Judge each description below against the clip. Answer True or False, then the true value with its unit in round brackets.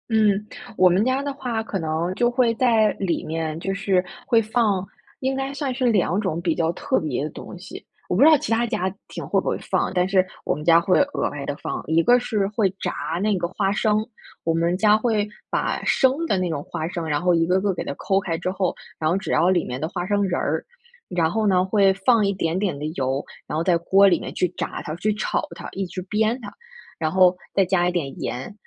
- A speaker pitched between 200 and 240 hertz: False (190 Hz)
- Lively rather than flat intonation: False (4.2 semitones)